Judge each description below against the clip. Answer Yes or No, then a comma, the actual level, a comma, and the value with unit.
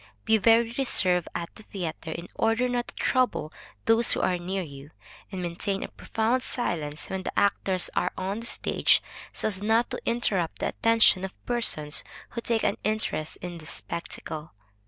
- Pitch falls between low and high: No, high, 195 Hz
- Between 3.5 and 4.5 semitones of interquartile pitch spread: No, average, 5.0 semitones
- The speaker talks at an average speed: Yes, average, 175 wpm